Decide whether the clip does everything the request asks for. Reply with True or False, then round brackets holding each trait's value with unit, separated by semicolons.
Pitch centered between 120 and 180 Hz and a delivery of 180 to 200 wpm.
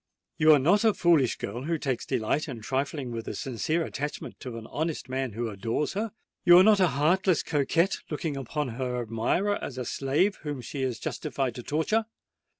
True (140 Hz; 190 wpm)